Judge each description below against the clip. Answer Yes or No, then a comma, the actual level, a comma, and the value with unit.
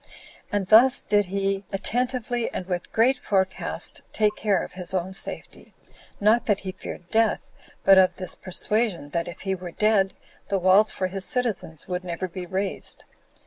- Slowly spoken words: No, average, 170 wpm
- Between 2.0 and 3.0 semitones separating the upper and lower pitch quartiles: Yes, average, 2.7 semitones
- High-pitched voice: Yes, high, 195 Hz